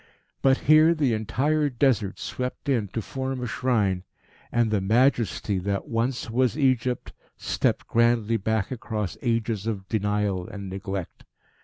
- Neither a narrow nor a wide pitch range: Yes, average, 3.9 semitones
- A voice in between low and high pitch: No, low, 115 Hz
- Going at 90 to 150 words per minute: Yes, average, 140 wpm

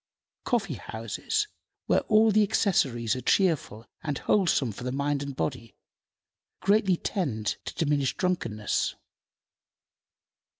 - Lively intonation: Yes, wide, 8.6 semitones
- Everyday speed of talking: No, slow, 110 wpm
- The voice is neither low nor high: Yes, medium, 145 Hz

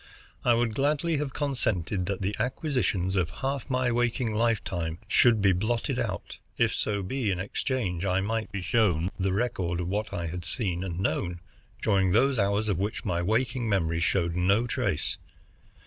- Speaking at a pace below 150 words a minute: No, average, 175 wpm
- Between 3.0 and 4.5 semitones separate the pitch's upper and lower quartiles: No, average, 4.9 semitones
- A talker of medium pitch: No, low, 100 Hz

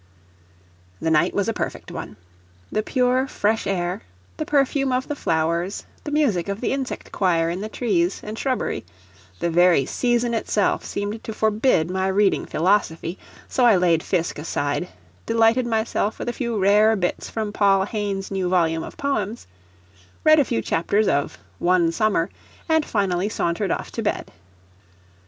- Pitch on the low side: No, high, 205 Hz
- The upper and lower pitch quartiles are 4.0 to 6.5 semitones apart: Yes, average, 4.6 semitones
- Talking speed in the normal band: Yes, average, 160 wpm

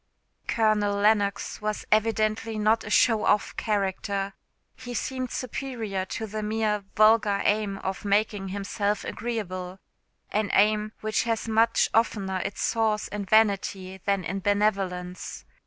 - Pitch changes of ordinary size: No, narrow, 1.8 semitones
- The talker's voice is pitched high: Yes, high, 210 Hz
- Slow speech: Yes, slow, 130 wpm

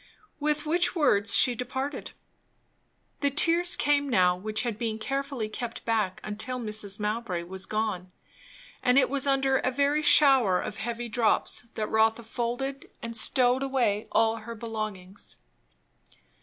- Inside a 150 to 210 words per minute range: No, average, 140 wpm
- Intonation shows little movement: No, average, 4.1 semitones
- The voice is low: No, high, 235 Hz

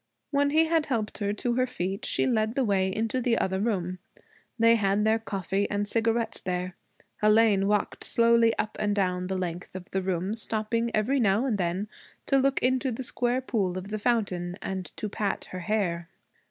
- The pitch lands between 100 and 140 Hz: No, high, 210 Hz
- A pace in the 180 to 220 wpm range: Yes, average, 195 wpm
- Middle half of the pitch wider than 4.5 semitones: No, average, 3.6 semitones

